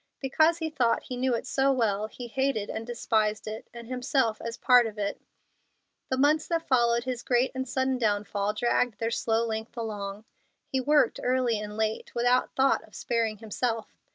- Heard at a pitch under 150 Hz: No, high, 235 Hz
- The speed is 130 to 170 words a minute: No, average, 180 wpm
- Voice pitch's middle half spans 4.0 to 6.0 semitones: No, average, 3.0 semitones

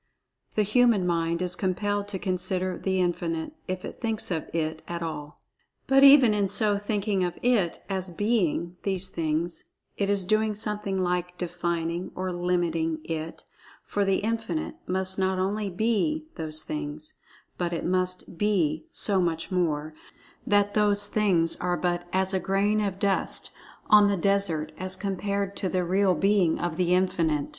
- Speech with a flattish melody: No, average, 3.0 semitones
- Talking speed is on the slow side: No, average, 165 wpm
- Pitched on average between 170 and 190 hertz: Yes, medium, 185 Hz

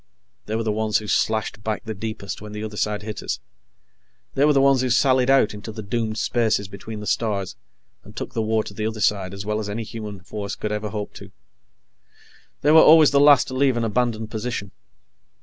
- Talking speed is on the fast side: Yes, fast, 220 wpm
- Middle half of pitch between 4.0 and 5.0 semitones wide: No, narrow, 2.4 semitones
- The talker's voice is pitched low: Yes, low, 110 Hz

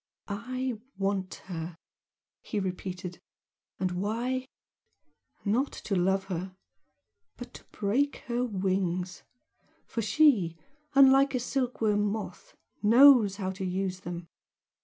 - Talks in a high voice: Yes, high, 200 Hz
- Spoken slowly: Yes, slow, 110 wpm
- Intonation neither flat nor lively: Yes, average, 4.9 semitones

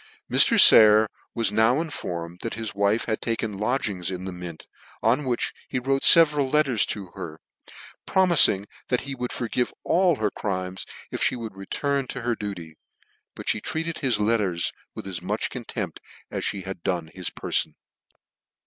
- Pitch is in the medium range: No, low, 110 Hz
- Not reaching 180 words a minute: Yes, average, 165 wpm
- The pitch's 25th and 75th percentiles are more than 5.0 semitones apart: Yes, wide, 5.4 semitones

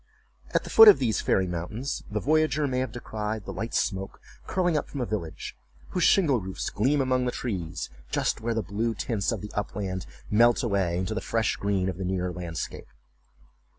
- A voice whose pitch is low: Yes, low, 110 Hz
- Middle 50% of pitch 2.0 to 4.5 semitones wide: No, average, 5.1 semitones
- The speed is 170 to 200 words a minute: Yes, average, 195 wpm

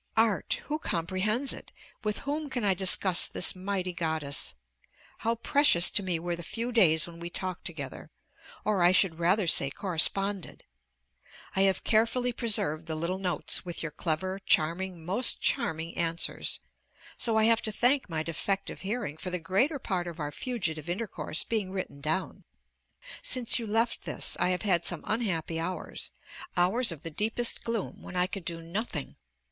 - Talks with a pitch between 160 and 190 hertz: Yes, medium, 185 Hz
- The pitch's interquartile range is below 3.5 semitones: No, average, 5.0 semitones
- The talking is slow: No, average, 170 wpm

